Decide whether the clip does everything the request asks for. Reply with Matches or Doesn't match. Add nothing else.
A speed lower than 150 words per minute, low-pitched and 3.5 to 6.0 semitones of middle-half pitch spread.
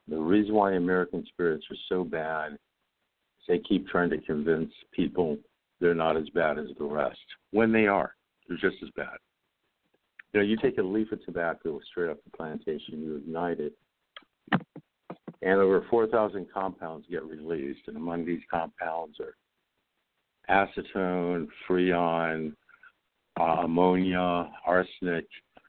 Doesn't match